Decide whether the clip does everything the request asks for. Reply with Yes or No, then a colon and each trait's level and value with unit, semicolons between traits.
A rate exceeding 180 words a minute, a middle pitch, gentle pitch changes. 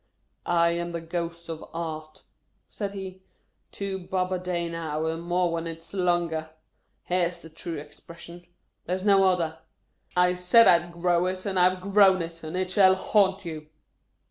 Yes: average, 190 wpm; medium, 175 Hz; narrow, 1.9 semitones